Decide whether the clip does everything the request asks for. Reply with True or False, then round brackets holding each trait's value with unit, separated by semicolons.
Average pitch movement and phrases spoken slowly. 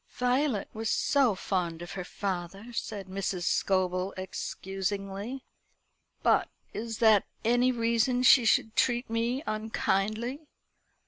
True (3.9 semitones; 115 wpm)